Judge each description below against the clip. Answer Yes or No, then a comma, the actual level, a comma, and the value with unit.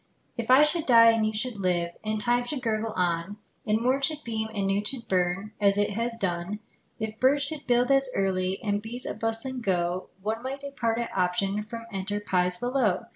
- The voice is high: Yes, high, 220 Hz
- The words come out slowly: No, fast, 205 wpm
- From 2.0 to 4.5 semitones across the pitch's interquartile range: Yes, average, 3.9 semitones